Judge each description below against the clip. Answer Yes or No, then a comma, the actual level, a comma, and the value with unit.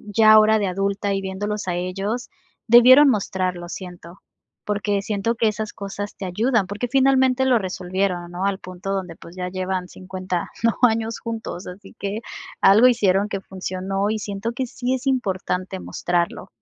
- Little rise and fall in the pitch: No, average, 3.3 semitones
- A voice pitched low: No, high, 200 Hz